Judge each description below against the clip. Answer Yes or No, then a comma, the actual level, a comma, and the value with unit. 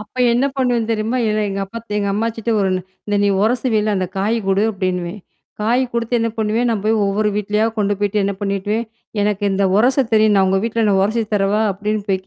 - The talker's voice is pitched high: Yes, high, 210 Hz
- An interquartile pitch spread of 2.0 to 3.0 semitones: Yes, narrow, 2.4 semitones